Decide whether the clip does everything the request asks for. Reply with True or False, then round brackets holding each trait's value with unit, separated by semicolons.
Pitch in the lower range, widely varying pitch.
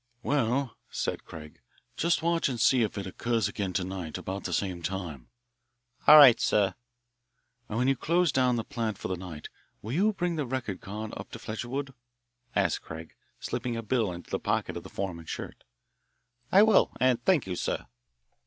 True (115 Hz; 6.2 semitones)